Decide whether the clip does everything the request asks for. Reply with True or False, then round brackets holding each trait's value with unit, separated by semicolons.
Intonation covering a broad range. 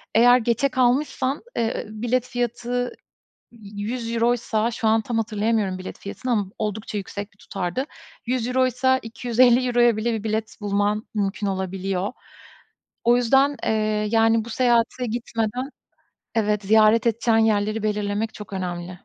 False (2.5 semitones)